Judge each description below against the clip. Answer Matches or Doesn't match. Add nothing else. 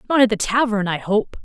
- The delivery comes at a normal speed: Doesn't match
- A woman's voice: Matches